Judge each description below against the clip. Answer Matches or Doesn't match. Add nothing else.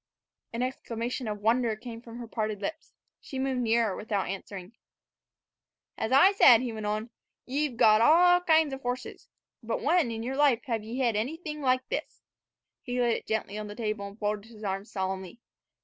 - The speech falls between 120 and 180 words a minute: Doesn't match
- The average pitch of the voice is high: Matches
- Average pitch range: Matches